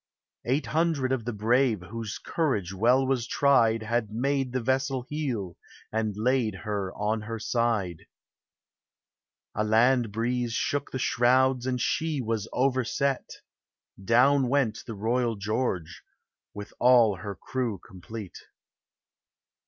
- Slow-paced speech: Yes, slow, 125 wpm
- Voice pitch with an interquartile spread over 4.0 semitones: No, average, 3.5 semitones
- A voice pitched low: Yes, low, 120 Hz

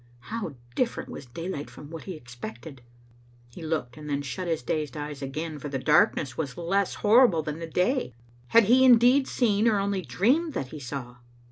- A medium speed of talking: Yes, average, 195 wpm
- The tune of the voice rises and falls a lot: Yes, wide, 6.6 semitones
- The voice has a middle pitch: Yes, medium, 160 Hz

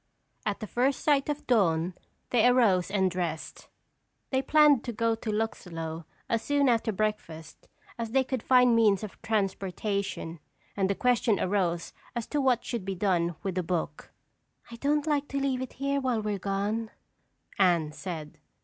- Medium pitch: No, high, 215 Hz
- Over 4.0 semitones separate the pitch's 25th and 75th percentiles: Yes, average, 5.2 semitones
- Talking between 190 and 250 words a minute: No, average, 165 wpm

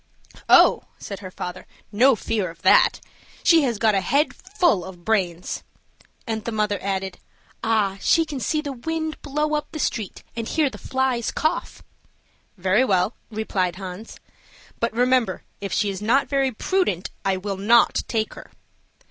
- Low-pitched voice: No, high, 220 Hz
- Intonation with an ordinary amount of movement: No, wide, 5.9 semitones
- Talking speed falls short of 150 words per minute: No, average, 165 wpm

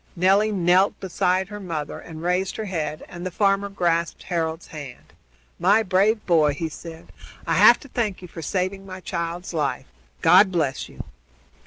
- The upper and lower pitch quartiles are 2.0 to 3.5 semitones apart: Yes, average, 2.9 semitones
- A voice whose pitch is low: No, medium, 180 Hz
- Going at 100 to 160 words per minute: No, average, 170 wpm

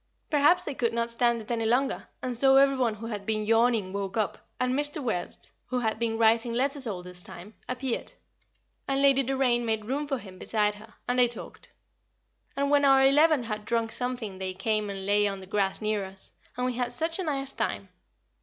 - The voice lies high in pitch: Yes, high, 235 Hz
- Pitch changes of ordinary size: Yes, average, 4.1 semitones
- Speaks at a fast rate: Yes, fast, 210 wpm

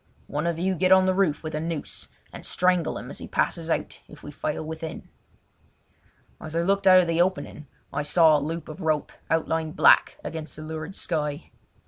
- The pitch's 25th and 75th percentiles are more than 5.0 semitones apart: No, narrow, 2.6 semitones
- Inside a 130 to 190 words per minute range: No, fast, 205 wpm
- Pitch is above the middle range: No, medium, 160 Hz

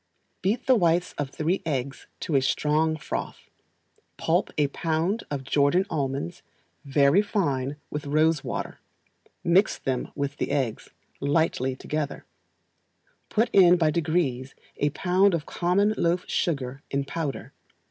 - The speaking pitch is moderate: Yes, medium, 155 Hz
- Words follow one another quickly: No, slow, 135 wpm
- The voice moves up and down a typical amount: Yes, average, 4.0 semitones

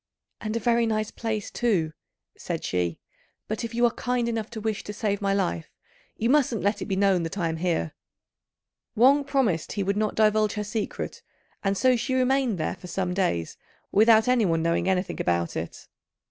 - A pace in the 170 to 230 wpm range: Yes, average, 190 wpm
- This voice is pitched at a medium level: No, high, 210 Hz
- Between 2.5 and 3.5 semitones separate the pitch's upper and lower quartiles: No, average, 4.2 semitones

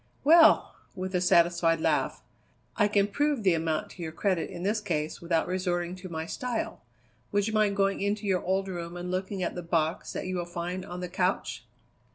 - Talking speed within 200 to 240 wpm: Yes, fast, 205 wpm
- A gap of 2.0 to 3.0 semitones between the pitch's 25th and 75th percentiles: Yes, narrow, 2.6 semitones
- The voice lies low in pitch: No, medium, 185 Hz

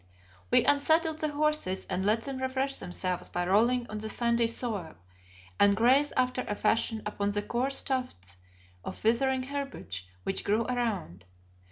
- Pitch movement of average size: Yes, average, 4.6 semitones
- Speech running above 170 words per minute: No, average, 155 wpm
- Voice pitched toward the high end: Yes, high, 235 Hz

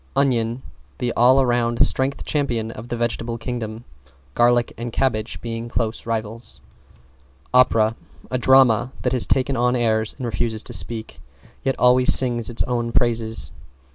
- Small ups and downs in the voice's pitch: Yes, narrow, 1.6 semitones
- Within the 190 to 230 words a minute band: No, average, 145 wpm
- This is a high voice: No, low, 120 Hz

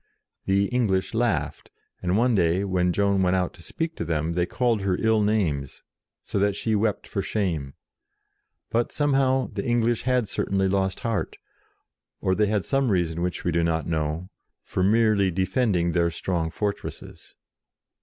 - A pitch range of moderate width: Yes, average, 4.1 semitones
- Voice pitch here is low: Yes, low, 100 Hz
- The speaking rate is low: No, average, 165 wpm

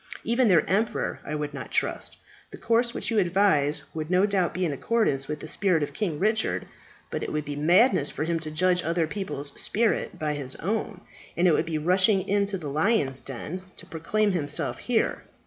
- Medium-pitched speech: Yes, medium, 175 Hz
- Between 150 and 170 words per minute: No, average, 200 wpm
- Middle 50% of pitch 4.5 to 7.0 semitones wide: Yes, average, 5.1 semitones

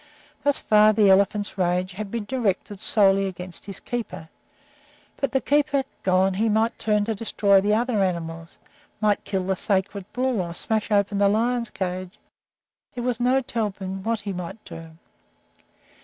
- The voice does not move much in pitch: No, average, 3.2 semitones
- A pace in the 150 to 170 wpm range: Yes, average, 160 wpm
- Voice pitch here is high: Yes, high, 205 Hz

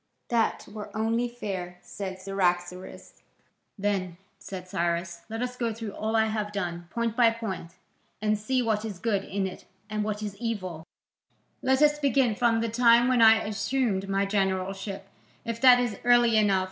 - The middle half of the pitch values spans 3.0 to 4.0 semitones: Yes, average, 3.3 semitones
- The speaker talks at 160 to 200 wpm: Yes, average, 170 wpm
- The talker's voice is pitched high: Yes, high, 215 Hz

